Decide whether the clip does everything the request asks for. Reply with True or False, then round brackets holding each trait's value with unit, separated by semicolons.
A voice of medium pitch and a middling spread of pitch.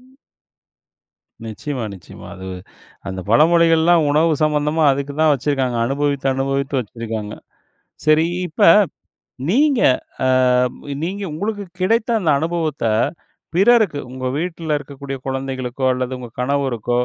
True (145 Hz; 4.1 semitones)